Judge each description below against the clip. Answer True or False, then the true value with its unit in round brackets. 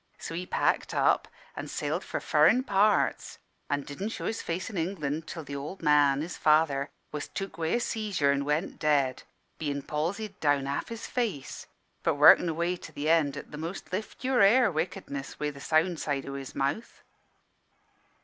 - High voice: False (155 Hz)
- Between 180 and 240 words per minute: True (185 wpm)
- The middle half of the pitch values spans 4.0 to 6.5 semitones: True (5.1 semitones)